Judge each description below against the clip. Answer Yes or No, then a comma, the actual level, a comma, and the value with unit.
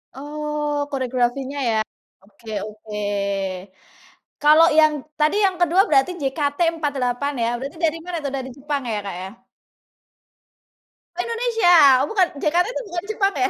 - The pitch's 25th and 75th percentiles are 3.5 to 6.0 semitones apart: Yes, average, 4.6 semitones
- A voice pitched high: Yes, very high, 295 Hz